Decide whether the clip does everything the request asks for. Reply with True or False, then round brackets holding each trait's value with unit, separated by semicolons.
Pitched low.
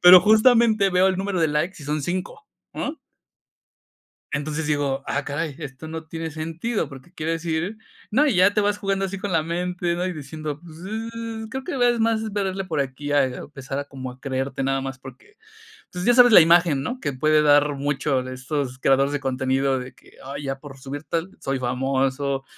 False (155 Hz)